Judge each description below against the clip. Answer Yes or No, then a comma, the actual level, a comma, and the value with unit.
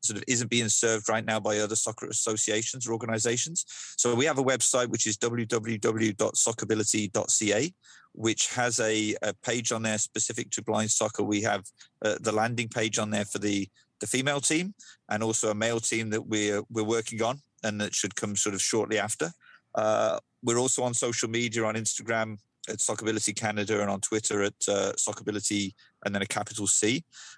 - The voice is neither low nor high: No, low, 110 Hz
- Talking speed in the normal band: Yes, average, 185 wpm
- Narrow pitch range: Yes, narrow, 1.9 semitones